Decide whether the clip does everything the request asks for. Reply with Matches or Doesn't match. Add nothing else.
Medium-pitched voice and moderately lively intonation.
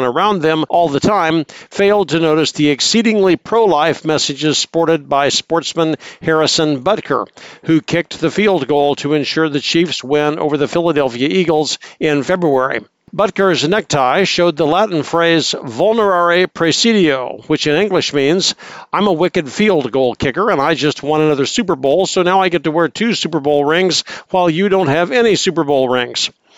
Matches